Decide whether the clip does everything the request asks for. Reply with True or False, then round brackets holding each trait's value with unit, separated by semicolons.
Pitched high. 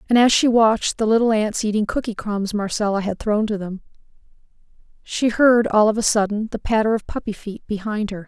True (215 Hz)